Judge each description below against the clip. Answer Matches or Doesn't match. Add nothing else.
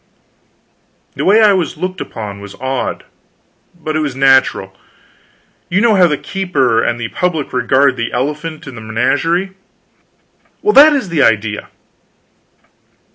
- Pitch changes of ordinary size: Doesn't match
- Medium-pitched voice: Matches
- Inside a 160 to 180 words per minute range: Doesn't match